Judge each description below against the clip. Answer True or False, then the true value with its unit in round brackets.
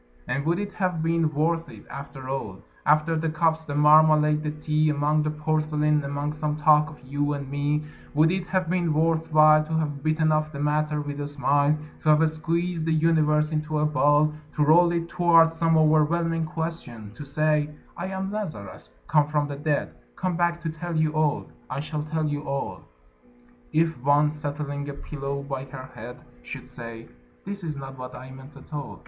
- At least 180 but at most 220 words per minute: True (195 wpm)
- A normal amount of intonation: False (1.8 semitones)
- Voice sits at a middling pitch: True (150 Hz)